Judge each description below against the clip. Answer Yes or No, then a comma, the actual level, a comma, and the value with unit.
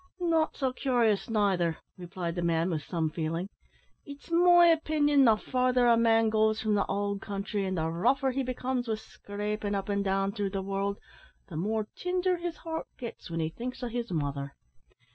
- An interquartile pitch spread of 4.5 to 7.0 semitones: Yes, average, 5.0 semitones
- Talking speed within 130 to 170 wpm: No, average, 185 wpm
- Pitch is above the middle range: Yes, high, 215 Hz